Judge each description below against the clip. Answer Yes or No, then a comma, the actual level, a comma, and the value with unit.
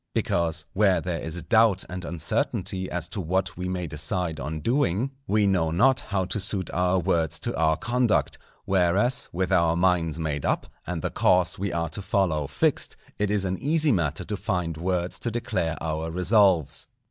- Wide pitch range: No, average, 3.3 semitones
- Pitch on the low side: Yes, very low, 90 Hz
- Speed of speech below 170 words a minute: No, average, 180 wpm